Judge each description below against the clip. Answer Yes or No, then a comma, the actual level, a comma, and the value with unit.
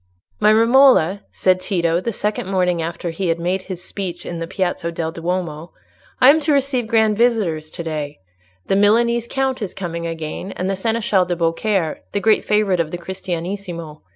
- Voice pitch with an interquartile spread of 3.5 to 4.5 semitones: Yes, average, 4.1 semitones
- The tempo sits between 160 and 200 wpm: Yes, average, 180 wpm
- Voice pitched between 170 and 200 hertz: Yes, medium, 185 Hz